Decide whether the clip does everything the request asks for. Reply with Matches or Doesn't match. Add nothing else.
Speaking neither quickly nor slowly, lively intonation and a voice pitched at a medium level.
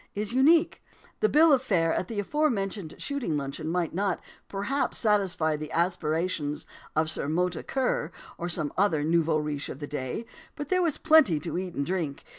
Matches